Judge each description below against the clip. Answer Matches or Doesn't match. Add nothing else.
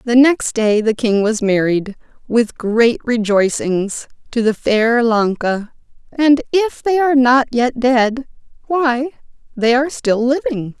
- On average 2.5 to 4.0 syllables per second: Matches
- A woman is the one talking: Matches